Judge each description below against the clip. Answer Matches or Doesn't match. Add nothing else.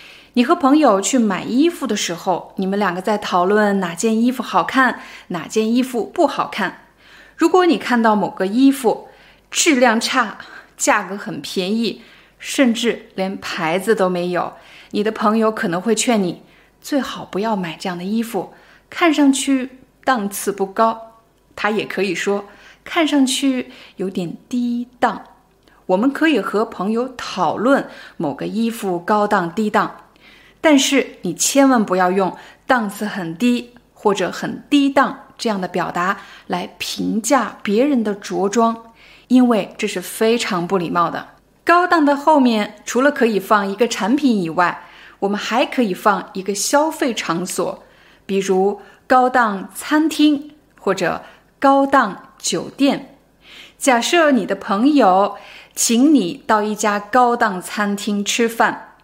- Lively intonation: Doesn't match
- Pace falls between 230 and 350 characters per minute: Doesn't match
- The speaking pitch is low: Doesn't match